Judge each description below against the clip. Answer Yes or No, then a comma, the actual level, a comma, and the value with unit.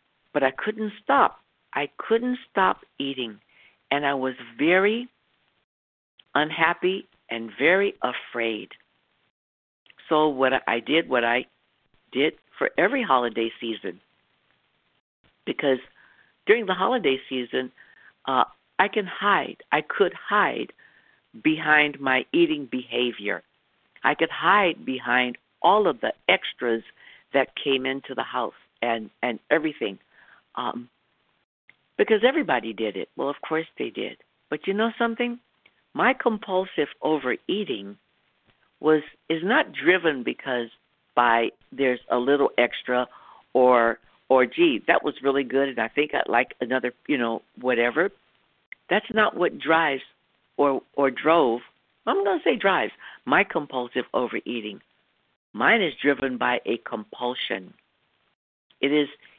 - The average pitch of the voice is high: No, low, 135 Hz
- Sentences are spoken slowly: Yes, slow, 125 wpm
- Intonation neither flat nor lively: No, wide, 7.0 semitones